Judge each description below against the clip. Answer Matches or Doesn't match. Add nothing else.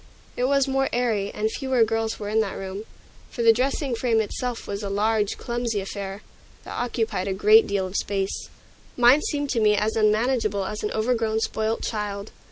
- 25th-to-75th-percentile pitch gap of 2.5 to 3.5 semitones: Matches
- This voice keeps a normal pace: Matches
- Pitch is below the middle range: Doesn't match